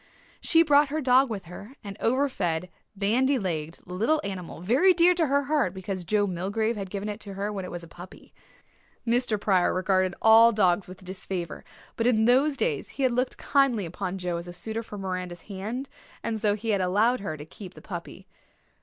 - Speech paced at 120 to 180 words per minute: No, fast, 205 wpm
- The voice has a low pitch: No, high, 205 Hz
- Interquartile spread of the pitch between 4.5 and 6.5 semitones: Yes, average, 5.2 semitones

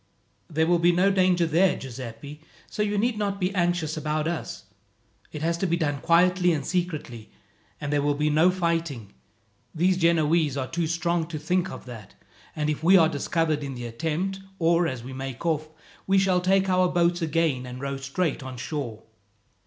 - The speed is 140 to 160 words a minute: No, average, 190 wpm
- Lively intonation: No, average, 3.7 semitones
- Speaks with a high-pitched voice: No, medium, 165 Hz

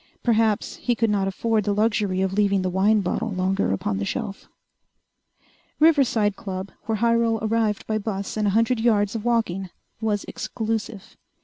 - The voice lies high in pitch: Yes, high, 210 Hz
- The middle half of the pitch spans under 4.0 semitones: Yes, narrow, 2.6 semitones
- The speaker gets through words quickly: No, average, 165 wpm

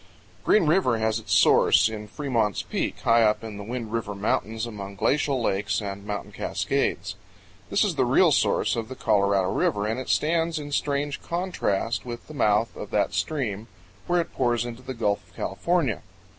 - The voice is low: Yes, low, 115 Hz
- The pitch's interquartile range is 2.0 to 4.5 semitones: No, average, 5.2 semitones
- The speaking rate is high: No, average, 185 wpm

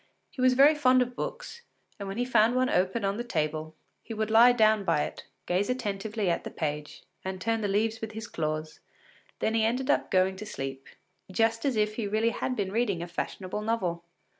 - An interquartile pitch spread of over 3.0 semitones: Yes, average, 4.0 semitones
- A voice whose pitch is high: Yes, high, 215 Hz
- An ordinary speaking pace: No, fast, 215 wpm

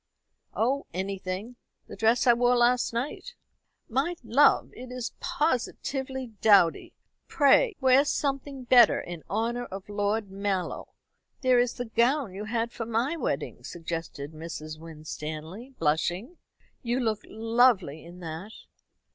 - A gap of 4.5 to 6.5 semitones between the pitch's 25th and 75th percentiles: Yes, wide, 5.4 semitones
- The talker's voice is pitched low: No, high, 230 Hz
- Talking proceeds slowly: Yes, slow, 130 wpm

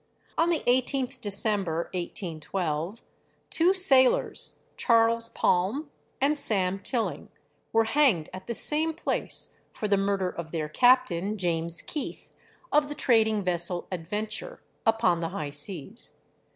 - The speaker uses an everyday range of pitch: No, wide, 6.6 semitones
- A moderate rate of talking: No, slow, 125 wpm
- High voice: Yes, high, 210 Hz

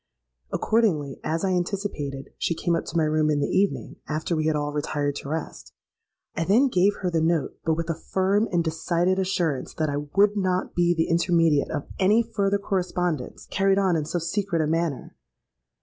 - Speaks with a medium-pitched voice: Yes, medium, 170 Hz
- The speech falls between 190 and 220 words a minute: Yes, average, 195 wpm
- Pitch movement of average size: Yes, average, 3.5 semitones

